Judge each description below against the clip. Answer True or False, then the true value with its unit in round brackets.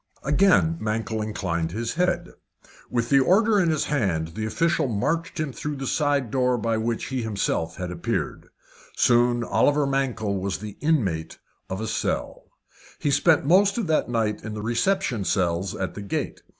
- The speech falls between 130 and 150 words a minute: False (165 wpm)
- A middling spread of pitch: False (6.3 semitones)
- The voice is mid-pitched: False (120 Hz)